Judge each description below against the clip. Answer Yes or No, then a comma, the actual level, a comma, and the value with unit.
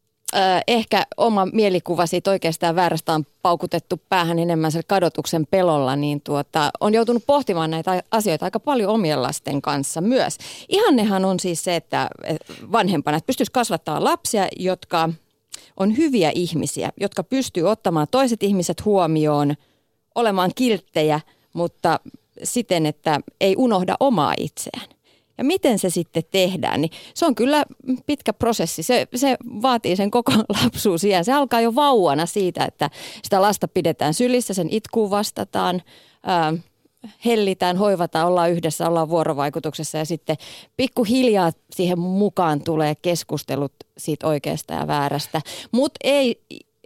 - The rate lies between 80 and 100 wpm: No, average, 135 wpm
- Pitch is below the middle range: No, medium, 180 Hz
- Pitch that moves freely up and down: Yes, wide, 5.9 semitones